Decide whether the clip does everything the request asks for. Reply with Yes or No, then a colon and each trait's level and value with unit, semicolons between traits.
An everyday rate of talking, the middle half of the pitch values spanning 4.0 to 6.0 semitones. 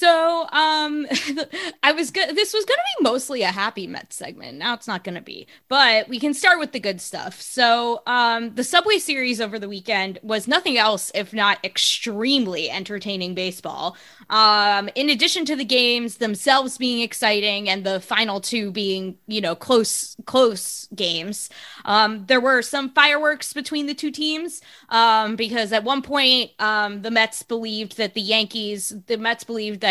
Yes: average, 180 wpm; wide, 5.5 semitones